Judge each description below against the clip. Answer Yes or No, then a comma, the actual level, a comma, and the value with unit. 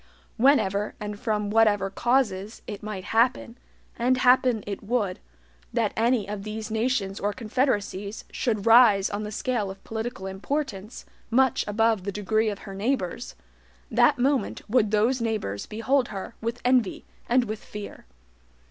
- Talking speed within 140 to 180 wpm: Yes, average, 150 wpm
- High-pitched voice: Yes, high, 220 Hz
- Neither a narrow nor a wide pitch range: Yes, average, 3.1 semitones